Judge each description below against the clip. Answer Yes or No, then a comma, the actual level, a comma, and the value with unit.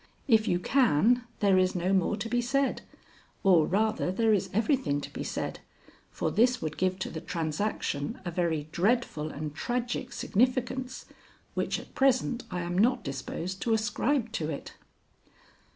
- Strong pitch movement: Yes, wide, 5.9 semitones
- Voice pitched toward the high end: Yes, high, 210 Hz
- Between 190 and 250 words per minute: No, average, 160 wpm